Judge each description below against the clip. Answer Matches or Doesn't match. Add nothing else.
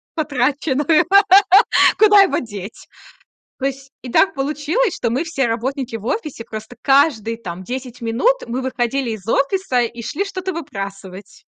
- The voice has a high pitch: Matches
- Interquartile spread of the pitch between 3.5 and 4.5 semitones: Doesn't match